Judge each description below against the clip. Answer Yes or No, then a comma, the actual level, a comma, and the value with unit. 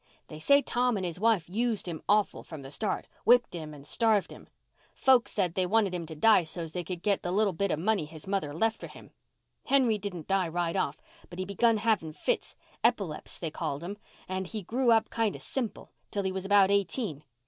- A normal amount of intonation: Yes, average, 4.7 semitones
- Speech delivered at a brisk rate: Yes, fast, 215 wpm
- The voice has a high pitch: Yes, high, 195 Hz